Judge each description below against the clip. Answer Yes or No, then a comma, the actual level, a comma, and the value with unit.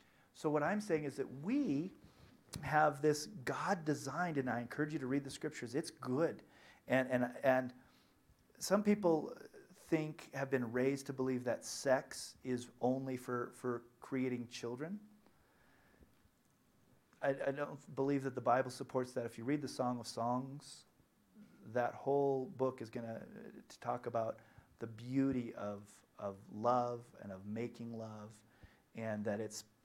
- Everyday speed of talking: Yes, average, 155 wpm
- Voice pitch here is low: Yes, low, 130 Hz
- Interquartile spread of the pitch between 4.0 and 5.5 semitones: No, average, 3.3 semitones